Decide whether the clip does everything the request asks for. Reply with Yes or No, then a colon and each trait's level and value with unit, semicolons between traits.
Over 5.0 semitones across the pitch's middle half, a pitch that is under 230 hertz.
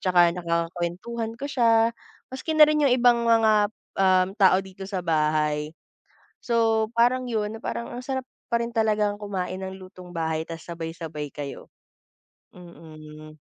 Yes: wide, 5.6 semitones; high, 190 Hz